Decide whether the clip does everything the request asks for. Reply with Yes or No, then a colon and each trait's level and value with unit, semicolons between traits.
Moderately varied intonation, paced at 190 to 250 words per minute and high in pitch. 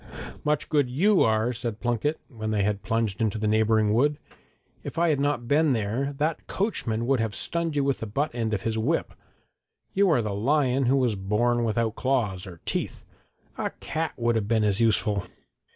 No: average, 4.7 semitones; average, 195 wpm; low, 115 Hz